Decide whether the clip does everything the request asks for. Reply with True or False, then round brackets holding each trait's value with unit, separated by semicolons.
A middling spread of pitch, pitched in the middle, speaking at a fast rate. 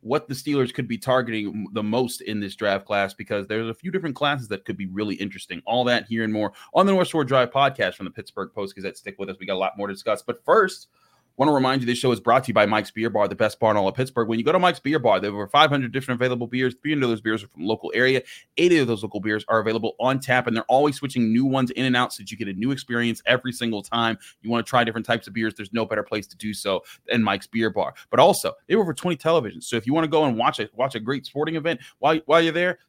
False (3.8 semitones; 120 Hz; 310 wpm)